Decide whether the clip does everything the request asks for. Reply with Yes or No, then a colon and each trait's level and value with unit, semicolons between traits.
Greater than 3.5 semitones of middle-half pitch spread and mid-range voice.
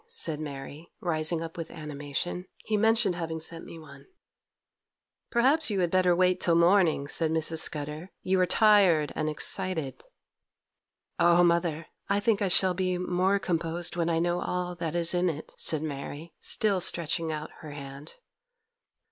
No: average, 2.7 semitones; medium, 170 Hz